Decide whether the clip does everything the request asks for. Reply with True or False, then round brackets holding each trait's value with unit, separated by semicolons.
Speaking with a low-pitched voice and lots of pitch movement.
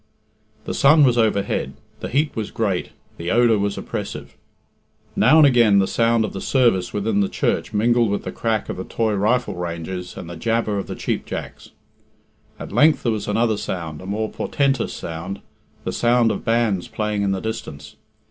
False (110 Hz; 3.5 semitones)